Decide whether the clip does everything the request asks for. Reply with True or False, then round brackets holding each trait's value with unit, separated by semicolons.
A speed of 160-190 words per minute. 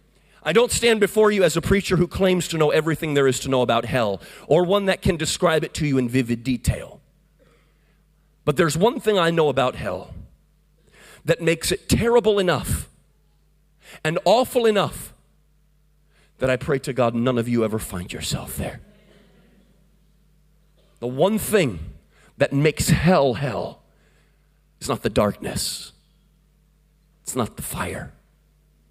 False (150 wpm)